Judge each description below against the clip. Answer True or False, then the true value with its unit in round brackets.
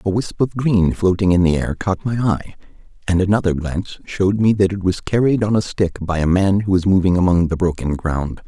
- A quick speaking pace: True (235 wpm)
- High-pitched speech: False (95 Hz)